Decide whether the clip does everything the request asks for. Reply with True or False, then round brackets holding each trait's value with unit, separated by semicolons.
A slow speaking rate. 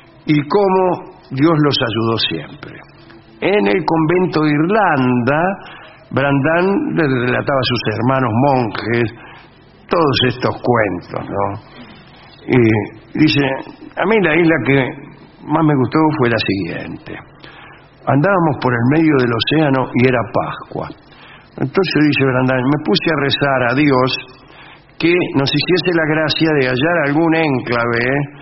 True (130 wpm)